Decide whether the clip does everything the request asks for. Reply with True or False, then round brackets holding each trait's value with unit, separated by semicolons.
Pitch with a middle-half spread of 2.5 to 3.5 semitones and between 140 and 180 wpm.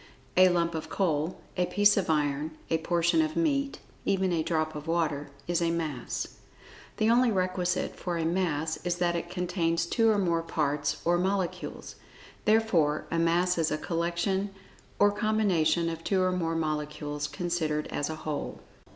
True (2.8 semitones; 170 wpm)